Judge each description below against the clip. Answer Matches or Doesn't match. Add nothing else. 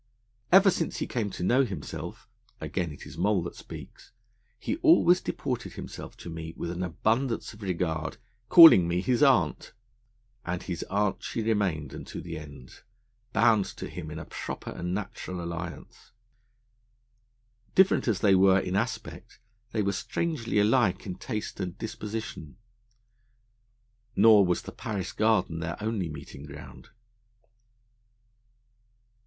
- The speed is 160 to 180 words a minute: Doesn't match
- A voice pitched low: Matches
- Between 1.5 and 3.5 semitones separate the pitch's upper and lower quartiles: Doesn't match